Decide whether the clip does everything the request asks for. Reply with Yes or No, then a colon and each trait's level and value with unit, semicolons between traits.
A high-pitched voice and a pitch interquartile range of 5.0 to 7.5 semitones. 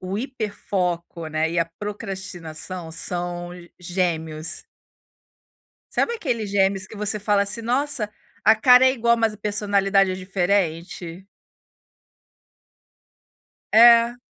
No: high, 195 Hz; average, 3.7 semitones